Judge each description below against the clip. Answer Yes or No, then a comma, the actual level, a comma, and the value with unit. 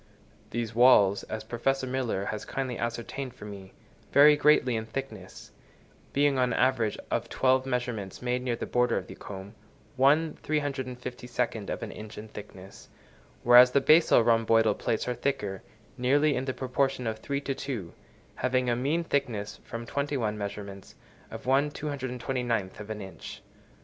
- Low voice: Yes, low, 125 Hz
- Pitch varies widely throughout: No, average, 3.5 semitones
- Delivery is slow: No, average, 155 wpm